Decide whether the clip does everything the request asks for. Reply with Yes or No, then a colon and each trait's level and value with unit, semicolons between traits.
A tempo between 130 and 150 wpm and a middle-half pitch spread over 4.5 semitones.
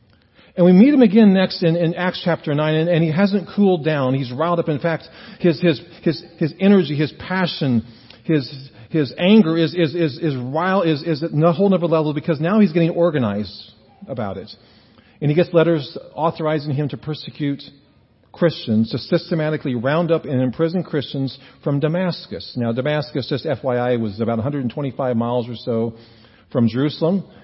No: average, 175 wpm; average, 5.0 semitones